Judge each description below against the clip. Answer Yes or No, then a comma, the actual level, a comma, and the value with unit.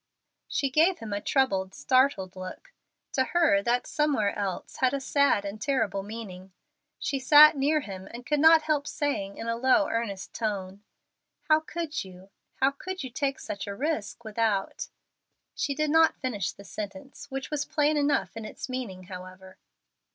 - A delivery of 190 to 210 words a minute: No, average, 175 wpm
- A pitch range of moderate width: No, wide, 6.6 semitones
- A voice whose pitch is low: No, very high, 255 Hz